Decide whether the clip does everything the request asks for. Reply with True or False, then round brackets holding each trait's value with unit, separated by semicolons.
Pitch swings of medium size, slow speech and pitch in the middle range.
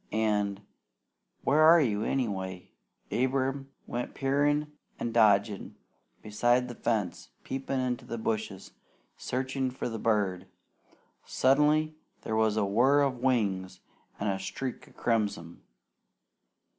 False (4.5 semitones; 120 wpm; 115 Hz)